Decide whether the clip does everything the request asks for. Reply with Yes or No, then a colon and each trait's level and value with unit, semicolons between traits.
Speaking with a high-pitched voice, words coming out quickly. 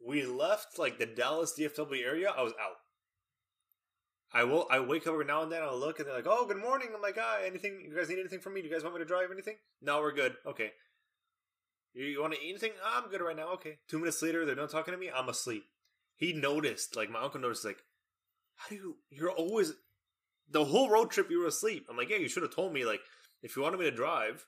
Yes: high, 195 Hz; fast, 255 wpm